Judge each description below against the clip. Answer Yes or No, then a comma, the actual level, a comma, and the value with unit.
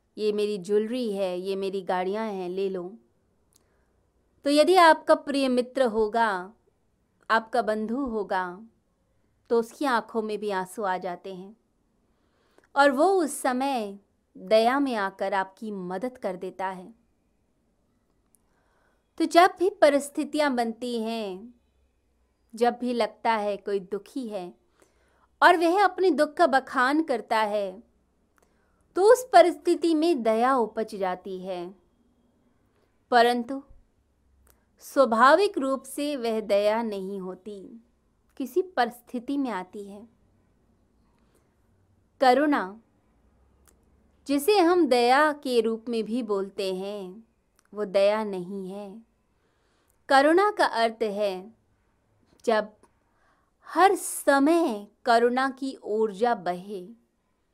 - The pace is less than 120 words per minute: Yes, slow, 110 wpm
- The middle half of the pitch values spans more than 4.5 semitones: Yes, wide, 5.6 semitones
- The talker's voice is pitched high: Yes, high, 225 Hz